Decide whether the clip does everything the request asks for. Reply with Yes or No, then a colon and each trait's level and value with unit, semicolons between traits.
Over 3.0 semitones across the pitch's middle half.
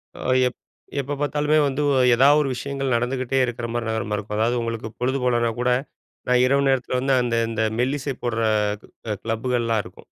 No: average, 2.7 semitones